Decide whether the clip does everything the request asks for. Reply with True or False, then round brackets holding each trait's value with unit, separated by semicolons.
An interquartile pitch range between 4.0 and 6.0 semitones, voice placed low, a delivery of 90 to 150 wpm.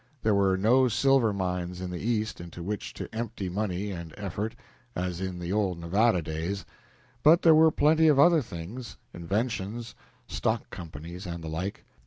False (4.8 semitones; 100 Hz; 170 wpm)